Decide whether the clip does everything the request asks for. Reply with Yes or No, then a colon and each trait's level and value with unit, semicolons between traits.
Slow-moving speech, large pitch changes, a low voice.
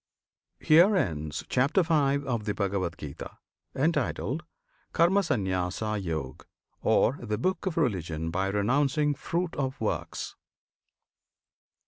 Yes: slow, 100 wpm; wide, 8.2 semitones; low, 125 Hz